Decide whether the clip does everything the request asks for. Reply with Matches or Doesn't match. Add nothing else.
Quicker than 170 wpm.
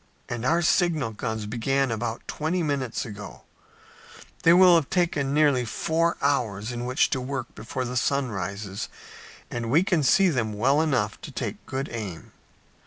Doesn't match